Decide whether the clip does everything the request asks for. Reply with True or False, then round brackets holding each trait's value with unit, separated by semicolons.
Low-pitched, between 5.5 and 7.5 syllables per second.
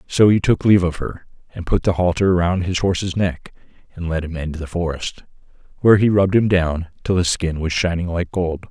True (90 Hz; 5.6 syllables/s)